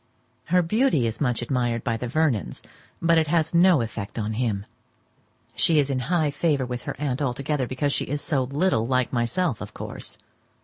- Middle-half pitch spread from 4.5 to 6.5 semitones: Yes, average, 4.9 semitones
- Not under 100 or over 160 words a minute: No, average, 185 wpm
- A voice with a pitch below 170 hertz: Yes, low, 135 Hz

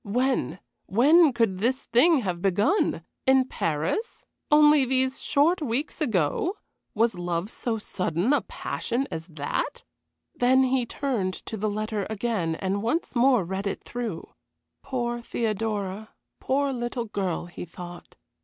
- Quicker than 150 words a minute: No, slow, 135 wpm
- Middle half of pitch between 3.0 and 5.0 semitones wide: No, wide, 5.6 semitones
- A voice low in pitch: No, high, 230 Hz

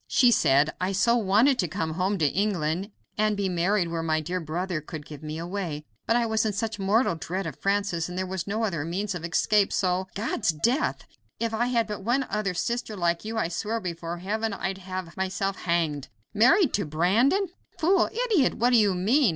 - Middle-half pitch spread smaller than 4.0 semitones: No, average, 4.5 semitones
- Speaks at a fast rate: Yes, fast, 210 wpm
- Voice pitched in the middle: No, high, 195 Hz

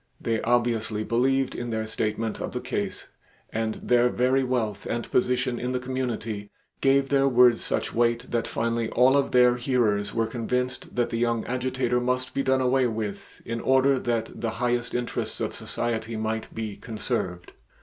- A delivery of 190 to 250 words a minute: No, average, 170 wpm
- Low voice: Yes, low, 120 Hz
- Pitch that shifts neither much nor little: No, narrow, 2.1 semitones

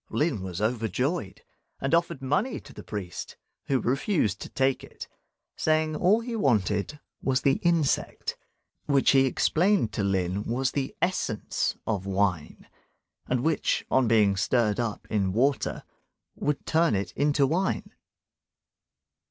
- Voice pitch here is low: Yes, low, 130 Hz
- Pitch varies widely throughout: Yes, wide, 7.0 semitones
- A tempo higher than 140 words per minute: No, slow, 135 wpm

